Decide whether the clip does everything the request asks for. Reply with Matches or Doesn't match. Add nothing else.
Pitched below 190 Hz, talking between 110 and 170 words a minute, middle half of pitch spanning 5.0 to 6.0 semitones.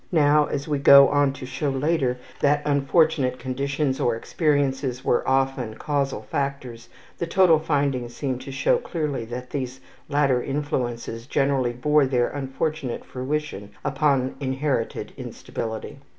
Doesn't match